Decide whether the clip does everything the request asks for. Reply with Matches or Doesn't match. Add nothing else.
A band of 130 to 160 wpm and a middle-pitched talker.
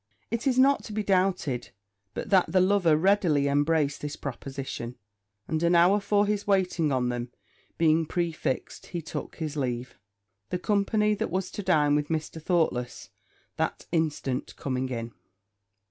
Matches